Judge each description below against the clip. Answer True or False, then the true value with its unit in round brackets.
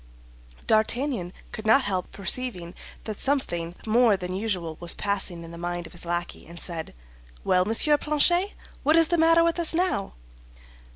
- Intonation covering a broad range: True (8.6 semitones)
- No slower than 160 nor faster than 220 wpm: True (165 wpm)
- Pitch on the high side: True (205 Hz)